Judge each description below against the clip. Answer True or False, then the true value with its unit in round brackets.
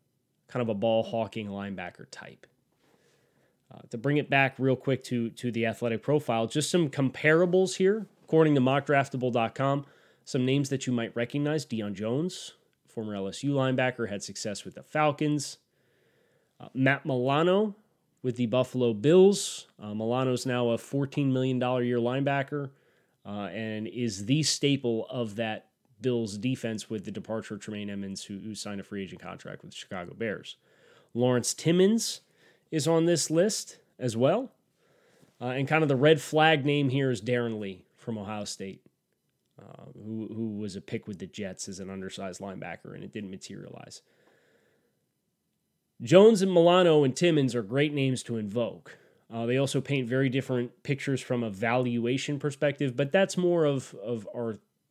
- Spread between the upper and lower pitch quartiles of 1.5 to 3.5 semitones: False (4.2 semitones)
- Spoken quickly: False (165 wpm)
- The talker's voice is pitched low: True (130 Hz)